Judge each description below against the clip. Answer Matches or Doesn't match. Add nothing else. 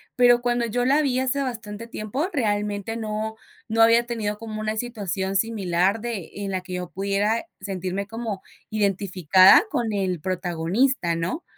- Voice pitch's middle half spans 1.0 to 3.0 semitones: Doesn't match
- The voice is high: Matches